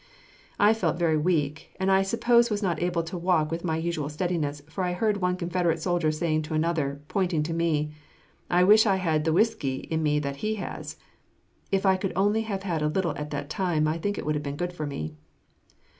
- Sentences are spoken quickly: Yes, fast, 220 wpm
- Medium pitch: Yes, medium, 170 Hz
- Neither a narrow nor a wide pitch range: Yes, average, 3.7 semitones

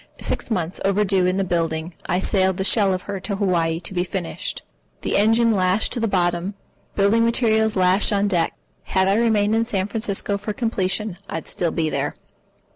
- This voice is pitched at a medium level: No, high, 195 Hz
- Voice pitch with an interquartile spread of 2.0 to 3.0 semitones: Yes, average, 2.7 semitones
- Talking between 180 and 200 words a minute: Yes, average, 190 wpm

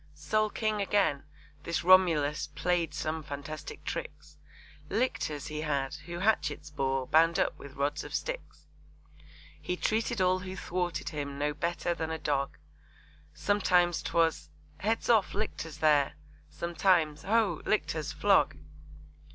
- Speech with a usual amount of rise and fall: Yes, average, 4.0 semitones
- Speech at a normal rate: No, slow, 130 wpm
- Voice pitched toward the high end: No, medium, 165 Hz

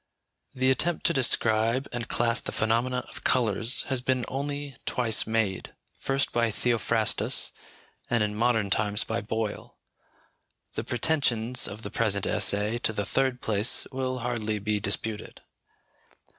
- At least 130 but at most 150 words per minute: Yes, average, 140 wpm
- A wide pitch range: No, average, 3.0 semitones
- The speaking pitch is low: Yes, low, 115 Hz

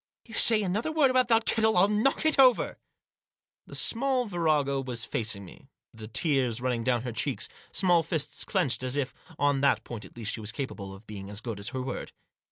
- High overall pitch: No, medium, 140 Hz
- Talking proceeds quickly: Yes, fast, 220 wpm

